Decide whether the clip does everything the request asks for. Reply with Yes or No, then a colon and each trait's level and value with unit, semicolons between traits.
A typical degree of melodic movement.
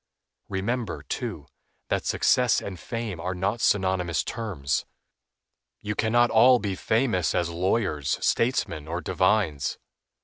Yes: average, 4.6 semitones